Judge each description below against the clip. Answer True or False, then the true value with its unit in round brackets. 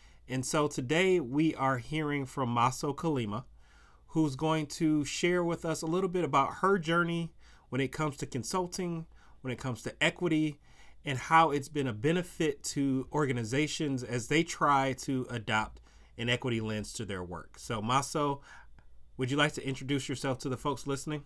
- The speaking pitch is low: False (145 Hz)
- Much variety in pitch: False (3.6 semitones)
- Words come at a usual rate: True (175 wpm)